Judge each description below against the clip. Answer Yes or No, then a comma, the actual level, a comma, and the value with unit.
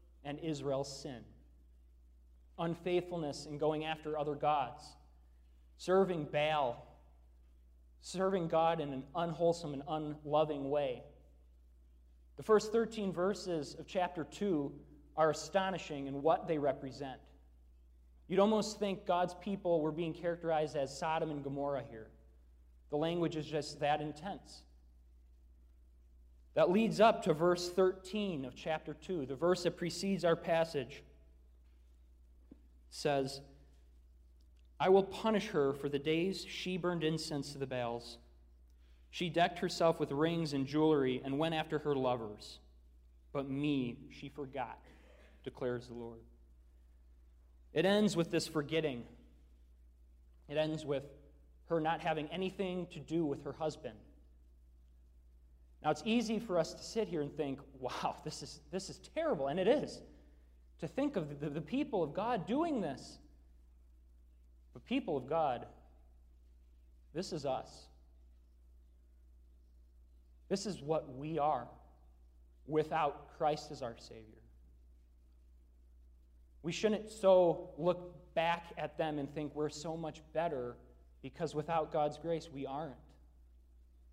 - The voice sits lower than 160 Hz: Yes, medium, 140 Hz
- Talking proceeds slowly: Yes, slow, 130 wpm